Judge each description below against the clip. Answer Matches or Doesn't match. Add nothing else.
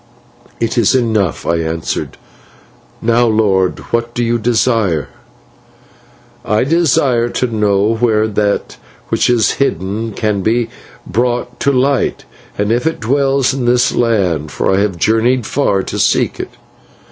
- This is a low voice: Matches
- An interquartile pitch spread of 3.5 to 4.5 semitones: Doesn't match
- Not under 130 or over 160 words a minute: Matches